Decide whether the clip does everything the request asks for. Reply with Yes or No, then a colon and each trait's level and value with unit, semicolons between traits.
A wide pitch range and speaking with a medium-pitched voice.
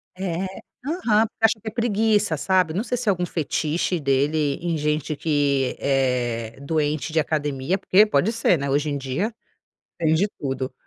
Yes: wide, 6.1 semitones; medium, 160 Hz